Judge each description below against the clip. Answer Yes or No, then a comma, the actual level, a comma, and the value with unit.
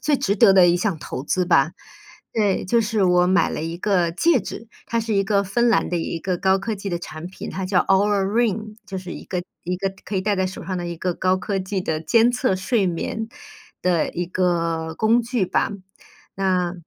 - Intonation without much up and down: No, average, 3.0 semitones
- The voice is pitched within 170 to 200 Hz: Yes, high, 190 Hz